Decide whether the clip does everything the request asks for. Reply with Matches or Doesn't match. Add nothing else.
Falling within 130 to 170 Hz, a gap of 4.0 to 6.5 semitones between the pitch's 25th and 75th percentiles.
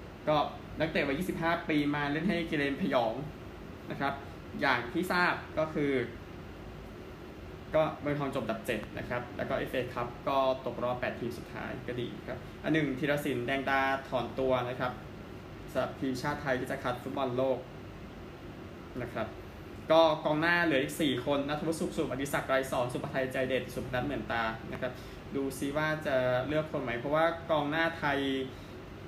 Doesn't match